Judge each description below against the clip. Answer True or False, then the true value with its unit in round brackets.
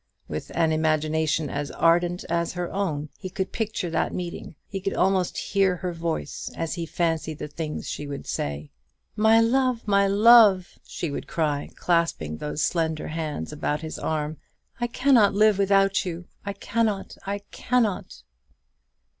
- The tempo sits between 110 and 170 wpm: True (155 wpm)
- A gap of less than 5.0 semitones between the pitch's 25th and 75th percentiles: True (4.2 semitones)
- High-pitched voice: False (175 Hz)